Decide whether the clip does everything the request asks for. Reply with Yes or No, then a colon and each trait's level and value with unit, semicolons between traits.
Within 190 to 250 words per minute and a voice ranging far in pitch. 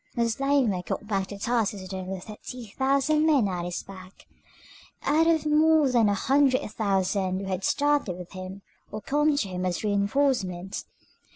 No: average, 165 wpm; wide, 6.6 semitones